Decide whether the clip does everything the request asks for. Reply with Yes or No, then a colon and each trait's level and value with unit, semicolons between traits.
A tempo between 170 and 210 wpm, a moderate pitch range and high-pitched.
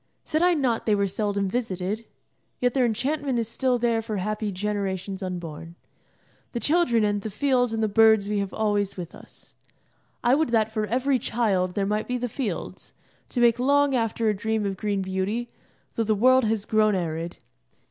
Yes: average, 190 wpm; average, 3.4 semitones; high, 220 Hz